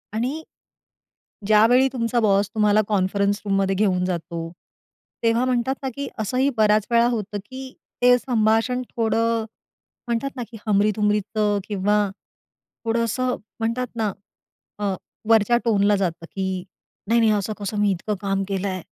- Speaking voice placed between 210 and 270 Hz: Yes, high, 215 Hz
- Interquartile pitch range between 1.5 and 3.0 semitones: Yes, narrow, 2.6 semitones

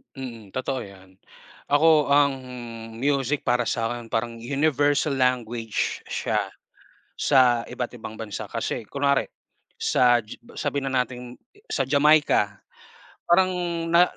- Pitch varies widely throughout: No, average, 3.6 semitones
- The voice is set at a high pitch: No, low, 125 Hz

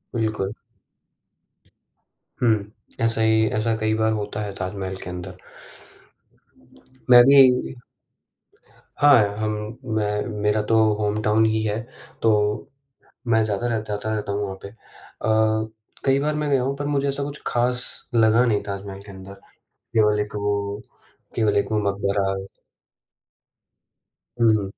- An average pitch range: No, narrow, 2.1 semitones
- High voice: No, low, 110 Hz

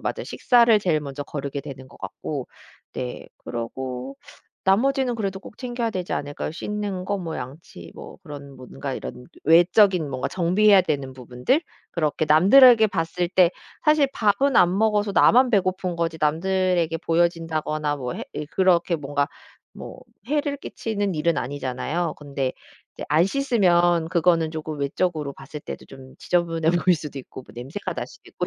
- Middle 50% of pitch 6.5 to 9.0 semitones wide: No, average, 5.3 semitones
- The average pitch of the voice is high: No, medium, 170 Hz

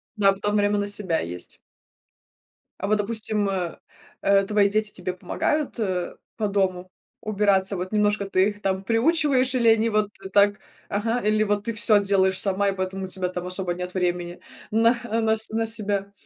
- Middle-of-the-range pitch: No, high, 205 Hz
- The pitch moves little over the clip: Yes, narrow, 2.2 semitones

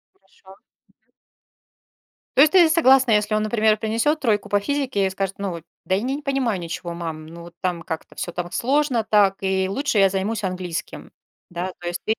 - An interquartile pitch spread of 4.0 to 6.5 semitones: Yes, average, 4.9 semitones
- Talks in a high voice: Yes, high, 200 Hz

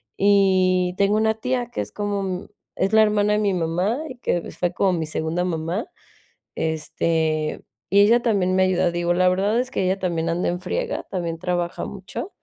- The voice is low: No, medium, 185 Hz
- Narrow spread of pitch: No, average, 3.1 semitones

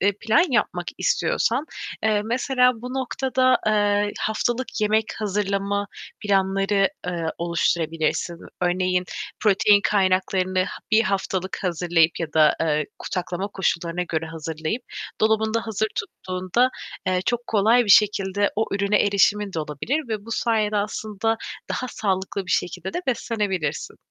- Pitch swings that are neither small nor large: Yes, average, 3.3 semitones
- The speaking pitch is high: Yes, high, 200 Hz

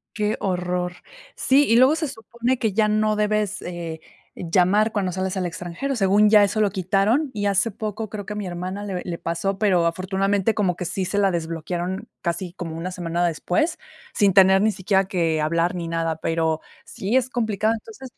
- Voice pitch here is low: No, high, 195 Hz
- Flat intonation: No, average, 3.3 semitones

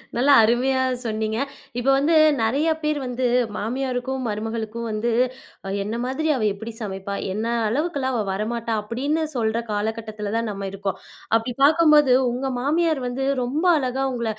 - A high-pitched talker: Yes, high, 240 Hz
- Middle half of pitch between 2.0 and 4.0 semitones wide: Yes, average, 3.7 semitones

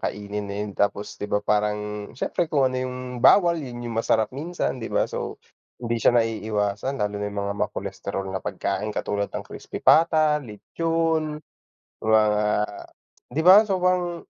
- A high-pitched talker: No, low, 115 Hz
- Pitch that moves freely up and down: Yes, wide, 7.1 semitones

